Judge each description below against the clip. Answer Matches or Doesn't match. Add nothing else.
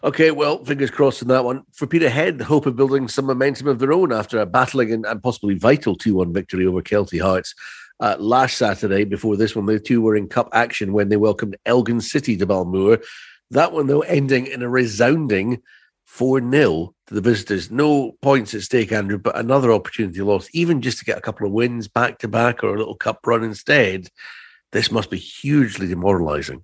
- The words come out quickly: Matches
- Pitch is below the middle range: Matches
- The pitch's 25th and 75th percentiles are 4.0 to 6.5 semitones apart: Matches